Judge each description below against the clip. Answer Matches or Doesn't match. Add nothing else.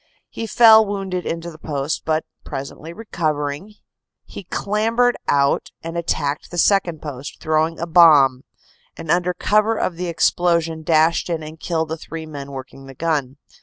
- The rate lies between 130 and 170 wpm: Matches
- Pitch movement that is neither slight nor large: Matches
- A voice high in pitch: Doesn't match